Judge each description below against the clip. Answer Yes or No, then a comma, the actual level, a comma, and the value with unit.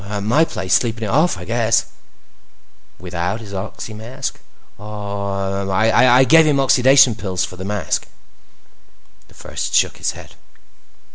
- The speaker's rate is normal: Yes, average, 145 wpm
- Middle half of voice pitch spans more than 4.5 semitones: No, average, 4.0 semitones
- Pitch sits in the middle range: No, low, 105 Hz